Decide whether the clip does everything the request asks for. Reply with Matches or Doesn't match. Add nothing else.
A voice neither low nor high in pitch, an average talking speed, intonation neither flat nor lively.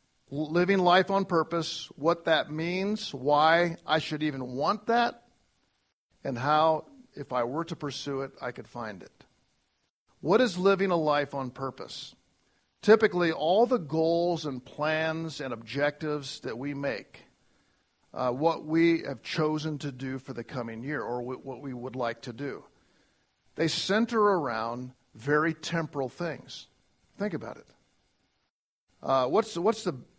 Matches